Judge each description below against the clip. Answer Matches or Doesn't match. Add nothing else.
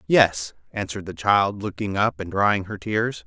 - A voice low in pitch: Matches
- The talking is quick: Doesn't match